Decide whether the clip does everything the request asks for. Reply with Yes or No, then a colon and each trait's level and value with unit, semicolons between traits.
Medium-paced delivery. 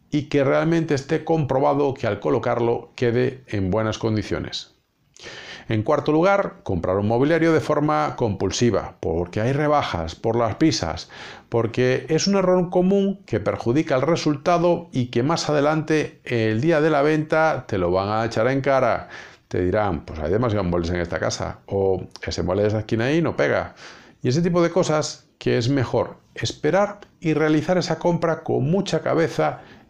Yes: average, 175 wpm